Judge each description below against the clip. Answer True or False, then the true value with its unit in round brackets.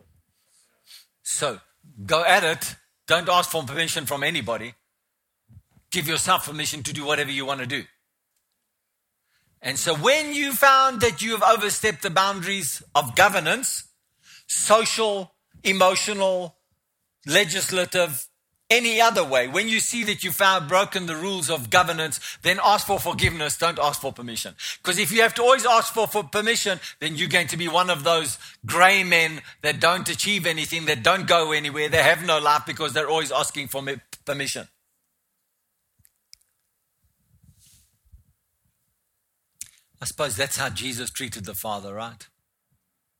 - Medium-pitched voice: True (165 Hz)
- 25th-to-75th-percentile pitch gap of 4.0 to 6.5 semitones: True (5.2 semitones)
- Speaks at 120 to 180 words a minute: True (145 wpm)